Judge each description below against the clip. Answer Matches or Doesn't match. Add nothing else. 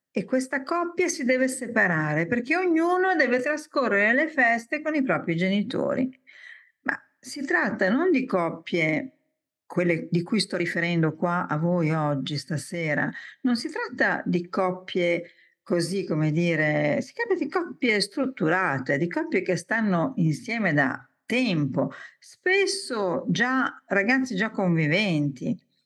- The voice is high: Matches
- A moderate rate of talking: Matches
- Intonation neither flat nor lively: Doesn't match